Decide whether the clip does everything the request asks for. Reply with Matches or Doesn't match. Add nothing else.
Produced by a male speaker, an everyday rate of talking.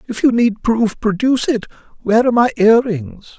Matches